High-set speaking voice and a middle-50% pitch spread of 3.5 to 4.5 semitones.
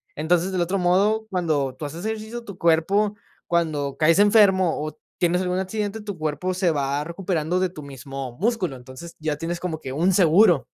No: medium, 175 Hz; average, 3.8 semitones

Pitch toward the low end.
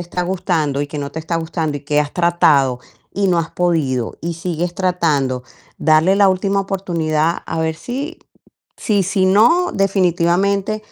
No: medium, 170 Hz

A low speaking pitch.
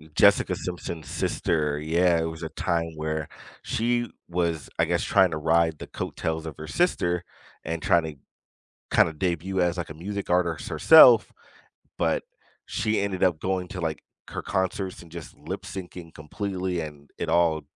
Yes: very low, 85 Hz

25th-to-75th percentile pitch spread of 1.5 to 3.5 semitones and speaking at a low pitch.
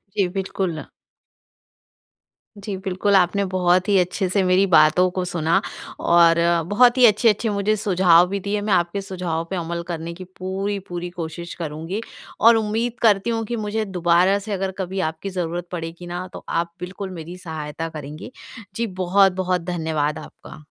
No: average, 2.7 semitones; medium, 185 Hz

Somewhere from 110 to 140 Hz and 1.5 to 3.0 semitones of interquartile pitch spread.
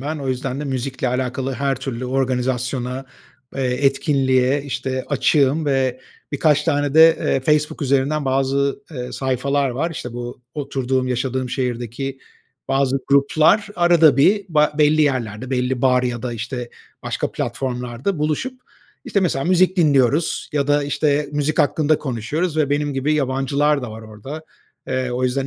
Yes: low, 135 Hz; average, 2.7 semitones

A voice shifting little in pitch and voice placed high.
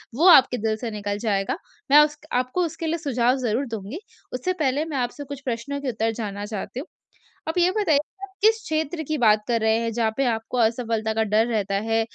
No: average, 4.9 semitones; high, 245 Hz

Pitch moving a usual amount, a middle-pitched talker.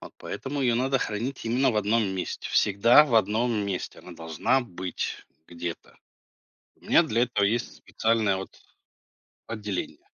No: average, 4.0 semitones; low, 110 Hz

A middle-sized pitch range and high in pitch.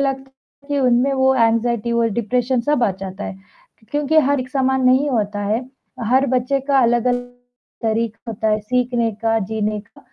Yes: average, 3.0 semitones; high, 240 Hz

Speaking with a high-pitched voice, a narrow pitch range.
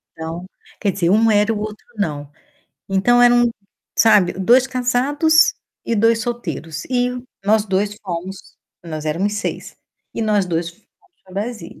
No: high, 210 Hz; average, 5.0 semitones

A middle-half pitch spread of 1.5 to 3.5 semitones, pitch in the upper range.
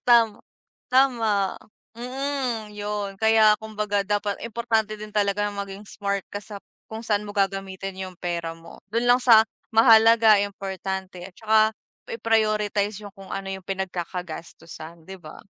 Yes: narrow, 2.4 semitones; high, 205 Hz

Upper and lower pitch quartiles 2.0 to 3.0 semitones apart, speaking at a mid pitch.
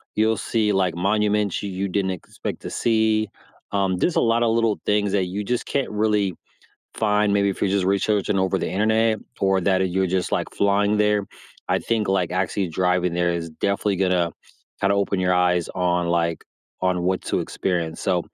No: narrow, 2.5 semitones; very low, 95 Hz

